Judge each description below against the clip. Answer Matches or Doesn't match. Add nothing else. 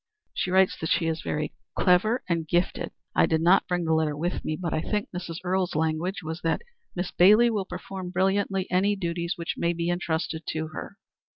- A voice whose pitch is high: Doesn't match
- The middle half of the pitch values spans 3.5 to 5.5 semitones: Doesn't match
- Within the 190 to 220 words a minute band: Matches